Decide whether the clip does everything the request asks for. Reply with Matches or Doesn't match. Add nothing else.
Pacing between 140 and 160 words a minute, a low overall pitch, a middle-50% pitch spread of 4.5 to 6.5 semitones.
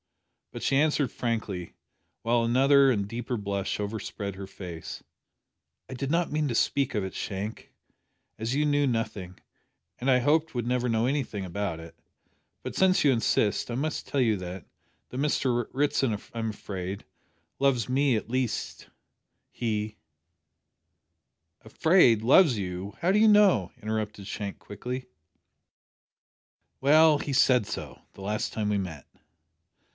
Matches